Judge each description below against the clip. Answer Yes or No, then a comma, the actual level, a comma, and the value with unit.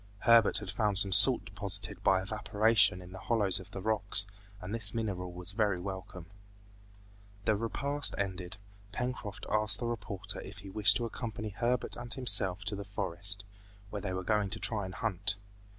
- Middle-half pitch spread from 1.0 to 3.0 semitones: Yes, narrow, 2.5 semitones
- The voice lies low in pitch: Yes, low, 100 Hz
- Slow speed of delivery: No, average, 175 wpm